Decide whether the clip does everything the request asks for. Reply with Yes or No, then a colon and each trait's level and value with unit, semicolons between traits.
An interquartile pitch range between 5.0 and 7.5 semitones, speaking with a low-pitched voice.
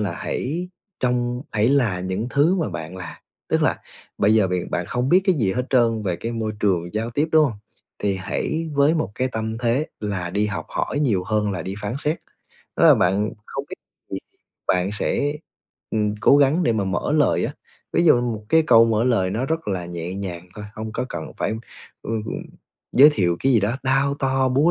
Yes: wide, 5.5 semitones; low, 115 Hz